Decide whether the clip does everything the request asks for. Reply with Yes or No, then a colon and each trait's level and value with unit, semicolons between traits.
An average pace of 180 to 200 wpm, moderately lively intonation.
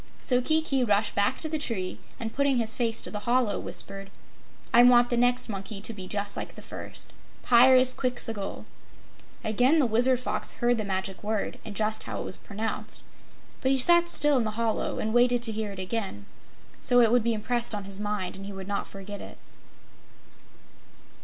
Yes: average, 190 wpm; average, 3.4 semitones